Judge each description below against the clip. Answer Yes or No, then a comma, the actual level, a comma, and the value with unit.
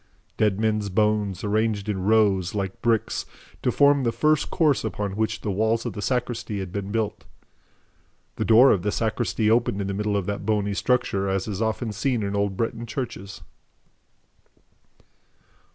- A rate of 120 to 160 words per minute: No, average, 170 wpm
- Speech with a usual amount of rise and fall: No, narrow, 2.3 semitones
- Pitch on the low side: Yes, low, 105 Hz